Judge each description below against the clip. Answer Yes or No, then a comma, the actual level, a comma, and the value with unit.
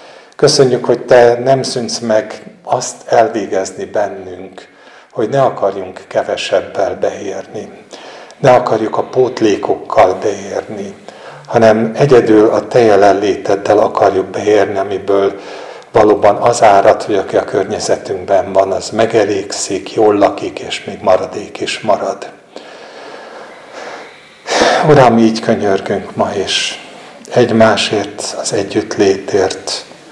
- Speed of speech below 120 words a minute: Yes, slow, 105 wpm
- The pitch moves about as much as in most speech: No, narrow, 1.8 semitones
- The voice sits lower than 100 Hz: No, low, 115 Hz